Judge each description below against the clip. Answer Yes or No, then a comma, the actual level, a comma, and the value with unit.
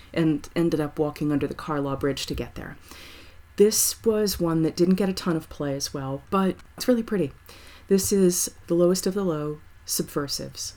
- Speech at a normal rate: Yes, average, 195 wpm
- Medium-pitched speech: Yes, medium, 155 Hz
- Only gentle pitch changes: No, average, 5.2 semitones